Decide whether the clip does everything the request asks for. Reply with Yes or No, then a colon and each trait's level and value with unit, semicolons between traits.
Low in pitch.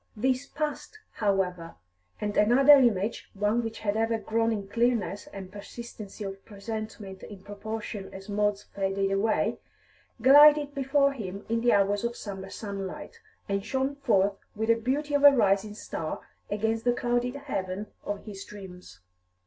No: high, 215 Hz